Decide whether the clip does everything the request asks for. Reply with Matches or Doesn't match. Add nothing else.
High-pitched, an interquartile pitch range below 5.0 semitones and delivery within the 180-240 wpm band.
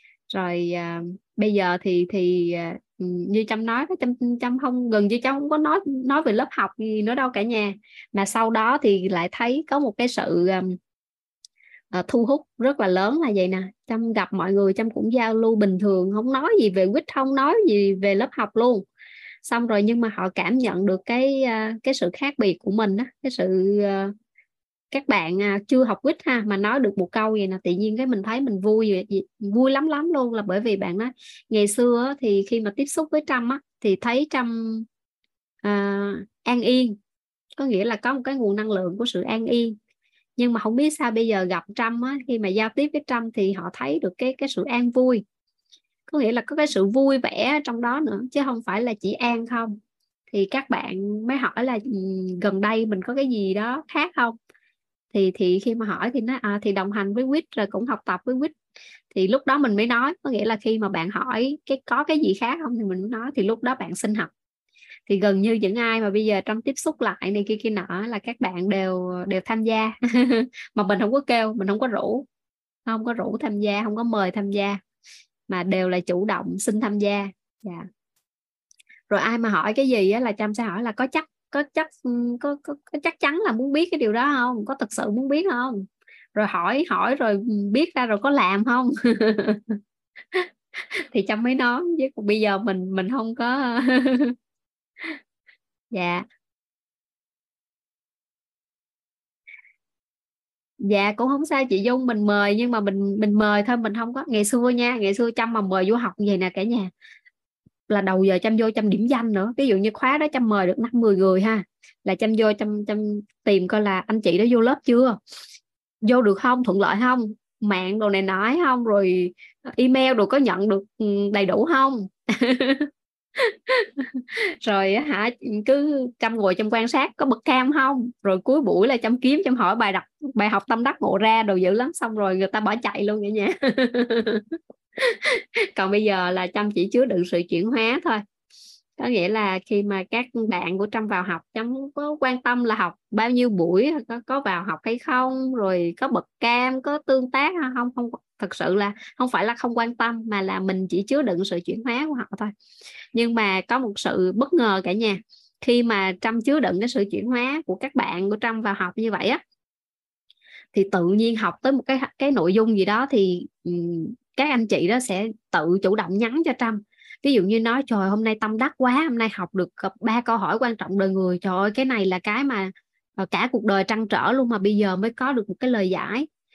Matches